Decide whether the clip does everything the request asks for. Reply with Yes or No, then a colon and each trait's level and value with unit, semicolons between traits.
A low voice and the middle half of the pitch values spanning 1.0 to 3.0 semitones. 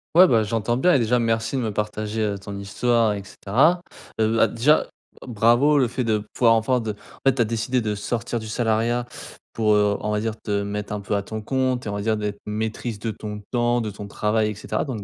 Yes: low, 110 Hz; narrow, 2.4 semitones